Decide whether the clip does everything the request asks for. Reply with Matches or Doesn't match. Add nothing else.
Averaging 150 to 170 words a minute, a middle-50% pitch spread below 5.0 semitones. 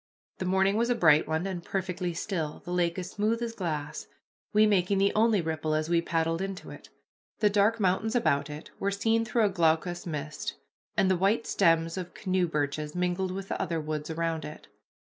Doesn't match